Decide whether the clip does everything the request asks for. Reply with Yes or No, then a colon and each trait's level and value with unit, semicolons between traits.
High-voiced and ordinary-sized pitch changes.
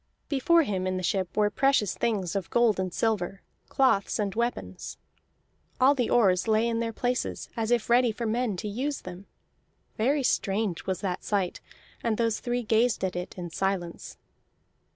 Yes: high, 215 Hz; average, 4.2 semitones